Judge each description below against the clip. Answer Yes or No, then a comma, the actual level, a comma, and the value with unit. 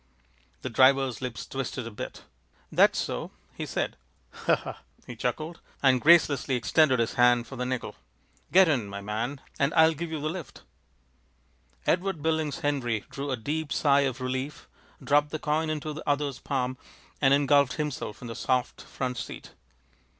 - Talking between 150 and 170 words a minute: Yes, average, 165 wpm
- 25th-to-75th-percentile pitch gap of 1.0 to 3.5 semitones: Yes, average, 3.2 semitones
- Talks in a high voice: No, low, 135 Hz